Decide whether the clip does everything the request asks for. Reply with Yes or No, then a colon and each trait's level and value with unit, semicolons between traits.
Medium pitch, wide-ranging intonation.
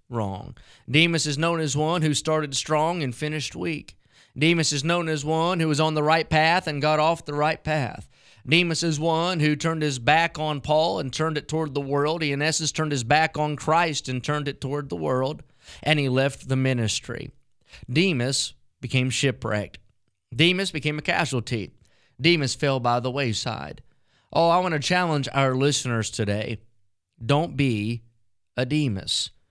No: medium, 145 Hz; average, 3.9 semitones